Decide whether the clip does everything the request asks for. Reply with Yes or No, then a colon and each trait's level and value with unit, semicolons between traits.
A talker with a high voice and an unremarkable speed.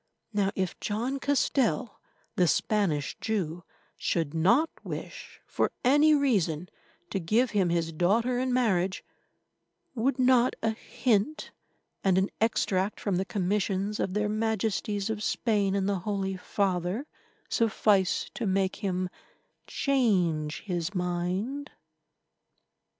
No: high, 200 Hz; slow, 120 wpm